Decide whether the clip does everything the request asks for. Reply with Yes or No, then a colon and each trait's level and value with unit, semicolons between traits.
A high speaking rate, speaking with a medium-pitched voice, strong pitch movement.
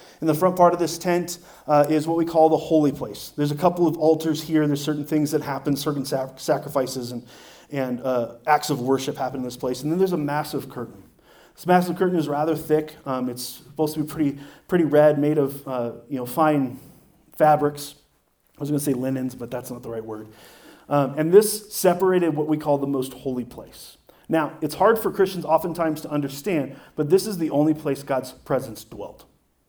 No: fast, 215 wpm; medium, 150 Hz; average, 3.2 semitones